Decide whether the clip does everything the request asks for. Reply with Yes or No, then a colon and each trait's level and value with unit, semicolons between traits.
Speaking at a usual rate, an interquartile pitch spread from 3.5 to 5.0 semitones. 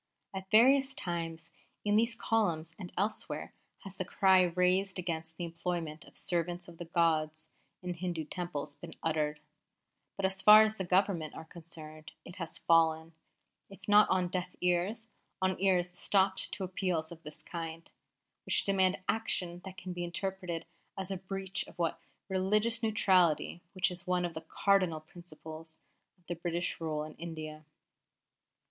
No: average, 155 wpm; average, 2.7 semitones